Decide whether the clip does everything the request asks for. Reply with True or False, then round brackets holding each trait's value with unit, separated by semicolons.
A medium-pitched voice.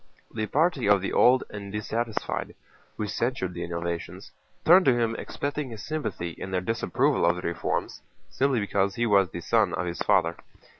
False (105 Hz)